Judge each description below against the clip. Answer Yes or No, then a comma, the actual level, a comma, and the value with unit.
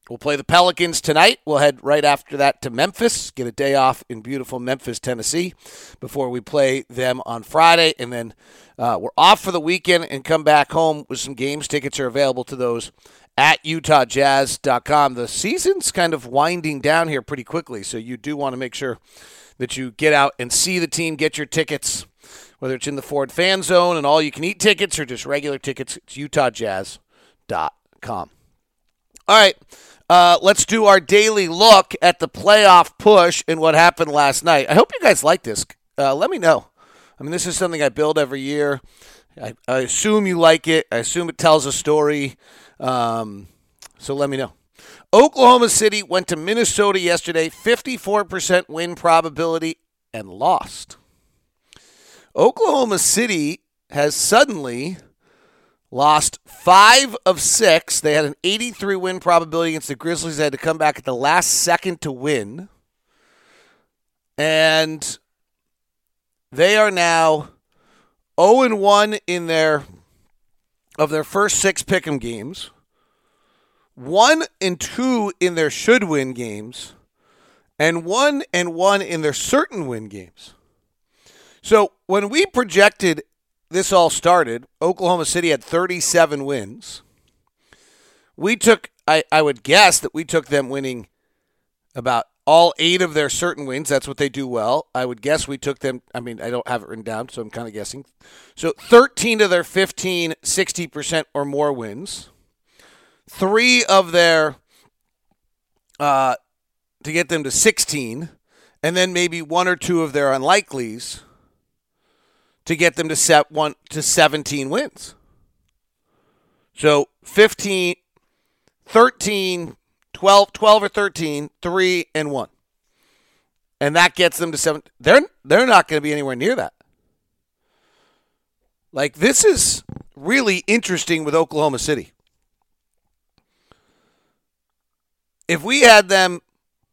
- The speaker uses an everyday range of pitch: Yes, average, 4.8 semitones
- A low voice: No, medium, 155 Hz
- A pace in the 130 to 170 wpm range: Yes, average, 150 wpm